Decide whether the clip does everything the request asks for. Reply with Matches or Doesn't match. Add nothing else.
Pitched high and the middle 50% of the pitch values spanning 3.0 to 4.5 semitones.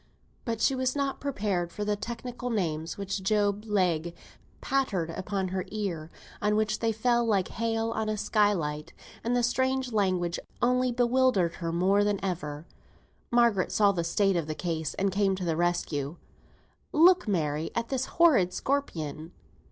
Doesn't match